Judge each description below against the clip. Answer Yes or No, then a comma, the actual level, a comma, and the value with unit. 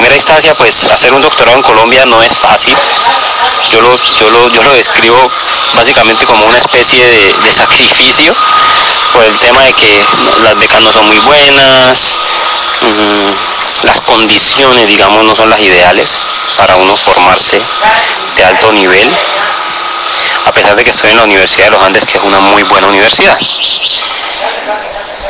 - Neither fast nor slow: Yes, average, 155 wpm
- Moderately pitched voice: No, low, 130 Hz